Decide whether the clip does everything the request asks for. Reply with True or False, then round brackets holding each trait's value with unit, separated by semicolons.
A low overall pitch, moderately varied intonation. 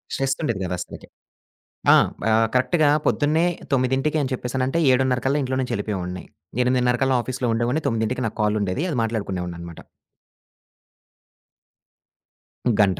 True (125 Hz; 4.1 semitones)